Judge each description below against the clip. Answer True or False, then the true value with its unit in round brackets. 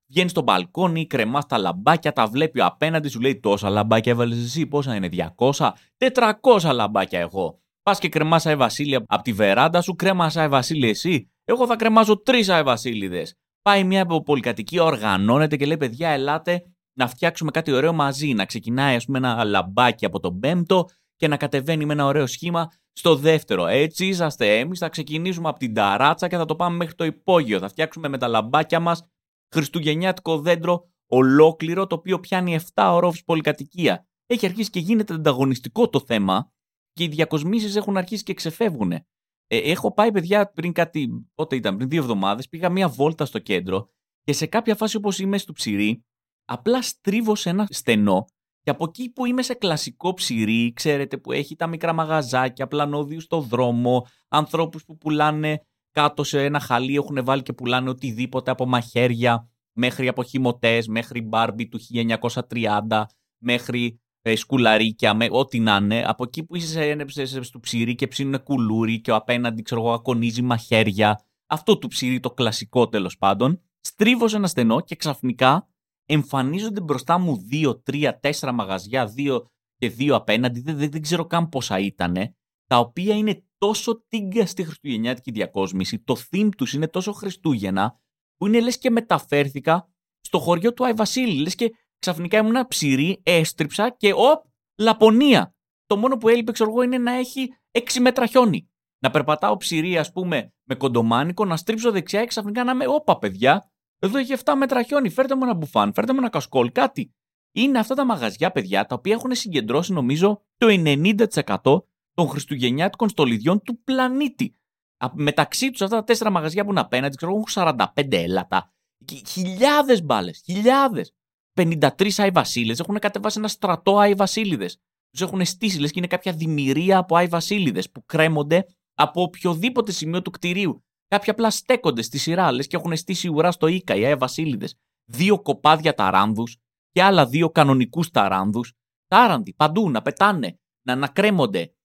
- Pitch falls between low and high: True (160 Hz)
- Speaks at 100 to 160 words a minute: False (170 wpm)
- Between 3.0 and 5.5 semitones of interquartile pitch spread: False (7.3 semitones)